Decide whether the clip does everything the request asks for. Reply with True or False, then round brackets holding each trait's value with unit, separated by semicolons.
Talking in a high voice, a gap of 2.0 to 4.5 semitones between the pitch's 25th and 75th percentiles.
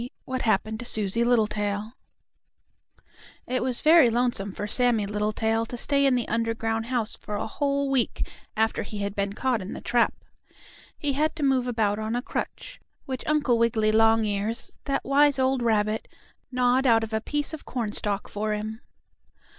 True (230 Hz; 3.1 semitones)